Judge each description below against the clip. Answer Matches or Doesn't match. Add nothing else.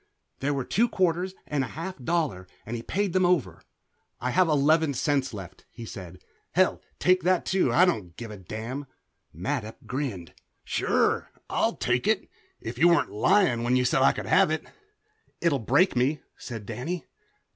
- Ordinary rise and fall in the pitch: Doesn't match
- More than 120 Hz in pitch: Matches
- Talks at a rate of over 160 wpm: Matches